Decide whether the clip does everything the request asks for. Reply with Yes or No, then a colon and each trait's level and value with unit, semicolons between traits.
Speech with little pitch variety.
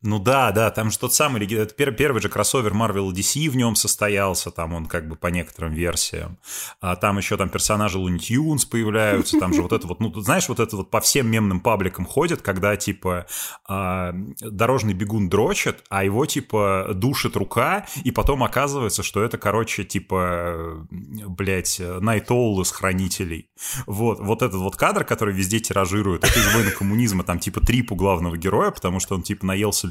No: average, 3.3 semitones